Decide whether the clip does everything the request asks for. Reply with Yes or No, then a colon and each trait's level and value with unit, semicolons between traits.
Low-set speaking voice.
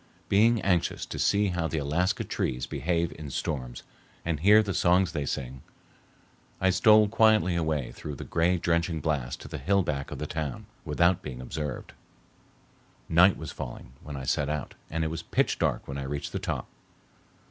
Yes: very low, 80 Hz